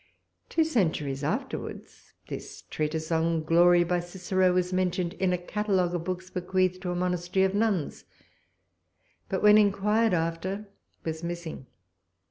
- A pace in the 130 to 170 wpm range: Yes, slow, 135 wpm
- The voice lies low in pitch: No, medium, 180 Hz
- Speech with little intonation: Yes, narrow, 2.0 semitones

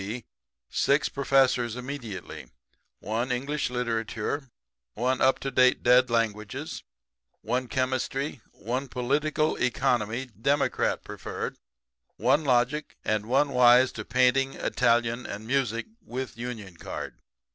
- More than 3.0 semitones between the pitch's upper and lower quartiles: No, narrow, 2.6 semitones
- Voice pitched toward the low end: Yes, low, 125 Hz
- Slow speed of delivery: Yes, slow, 115 wpm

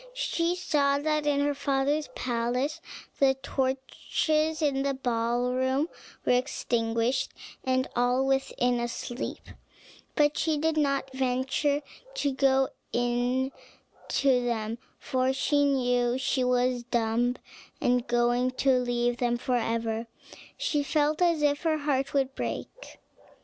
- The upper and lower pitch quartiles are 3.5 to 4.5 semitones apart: No, average, 2.8 semitones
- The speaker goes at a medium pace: No, slow, 120 wpm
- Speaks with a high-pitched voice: Yes, very high, 260 Hz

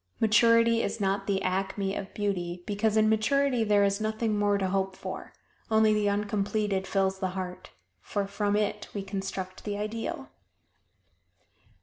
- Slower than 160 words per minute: Yes, average, 150 wpm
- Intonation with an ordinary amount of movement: No, narrow, 1.9 semitones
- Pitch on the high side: Yes, high, 205 Hz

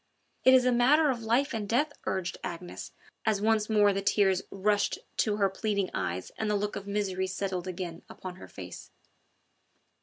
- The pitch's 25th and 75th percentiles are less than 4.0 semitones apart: Yes, average, 2.9 semitones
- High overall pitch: Yes, high, 205 Hz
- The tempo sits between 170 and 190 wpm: Yes, average, 180 wpm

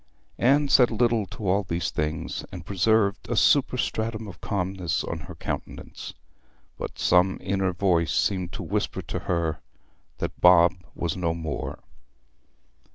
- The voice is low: Yes, very low, 90 Hz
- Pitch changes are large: No, average, 3.6 semitones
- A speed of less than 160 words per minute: Yes, average, 140 wpm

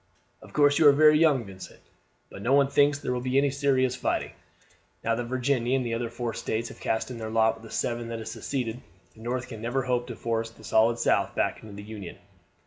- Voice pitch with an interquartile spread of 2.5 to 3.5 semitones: Yes, average, 2.9 semitones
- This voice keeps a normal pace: No, fast, 235 wpm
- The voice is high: No, low, 120 Hz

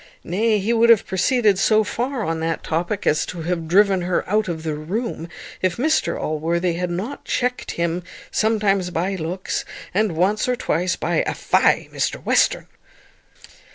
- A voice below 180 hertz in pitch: No, medium, 185 Hz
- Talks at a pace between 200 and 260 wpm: No, average, 165 wpm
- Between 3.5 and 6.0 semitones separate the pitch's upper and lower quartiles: Yes, average, 4.3 semitones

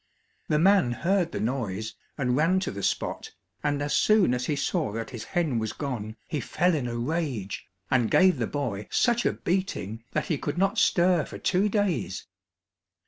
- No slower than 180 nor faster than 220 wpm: Yes, average, 190 wpm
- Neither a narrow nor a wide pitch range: No, wide, 7.4 semitones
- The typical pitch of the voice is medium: Yes, medium, 145 Hz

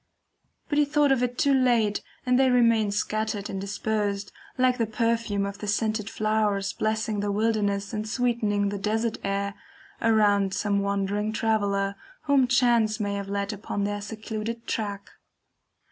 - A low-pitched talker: No, high, 215 Hz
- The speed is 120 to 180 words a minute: Yes, average, 155 wpm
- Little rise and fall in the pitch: Yes, narrow, 2.3 semitones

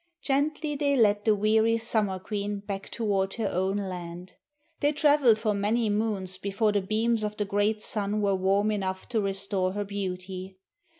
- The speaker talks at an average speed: Yes, average, 170 wpm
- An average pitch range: No, narrow, 2.3 semitones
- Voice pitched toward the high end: Yes, high, 205 Hz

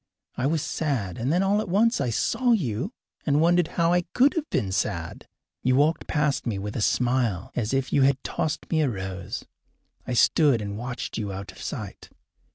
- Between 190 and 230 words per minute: Yes, average, 200 wpm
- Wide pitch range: Yes, wide, 7.1 semitones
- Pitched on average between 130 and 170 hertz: Yes, low, 135 Hz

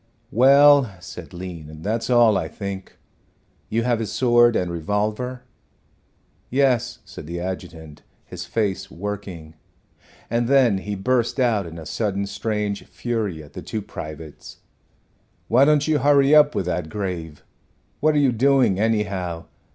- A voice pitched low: Yes, low, 105 Hz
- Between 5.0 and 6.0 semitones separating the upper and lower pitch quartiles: Yes, wide, 5.4 semitones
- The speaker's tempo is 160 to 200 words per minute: No, average, 145 wpm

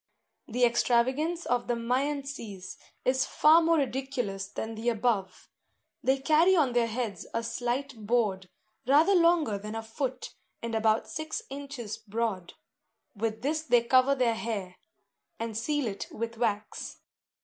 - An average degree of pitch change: Yes, average, 3.8 semitones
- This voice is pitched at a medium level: No, high, 240 Hz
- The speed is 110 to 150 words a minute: Yes, average, 140 wpm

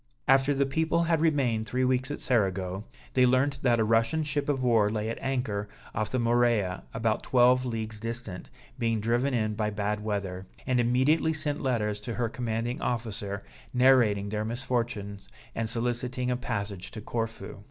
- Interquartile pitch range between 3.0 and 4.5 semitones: Yes, average, 3.3 semitones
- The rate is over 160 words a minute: Yes, average, 170 wpm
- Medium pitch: No, low, 115 Hz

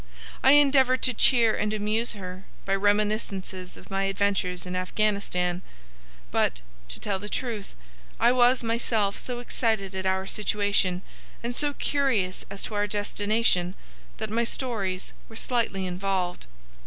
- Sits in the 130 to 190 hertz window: No, high, 205 Hz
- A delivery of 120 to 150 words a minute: Yes, average, 140 wpm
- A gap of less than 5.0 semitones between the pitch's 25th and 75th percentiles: Yes, average, 3.5 semitones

